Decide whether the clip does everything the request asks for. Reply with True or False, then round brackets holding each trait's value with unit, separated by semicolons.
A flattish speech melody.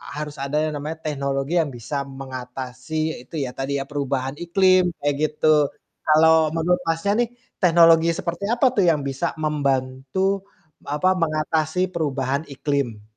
False (3.5 semitones)